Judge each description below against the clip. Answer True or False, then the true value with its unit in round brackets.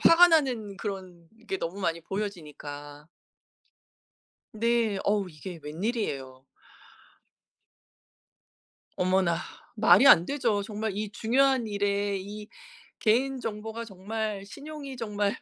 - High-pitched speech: True (205 Hz)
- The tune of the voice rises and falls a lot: False (3.7 semitones)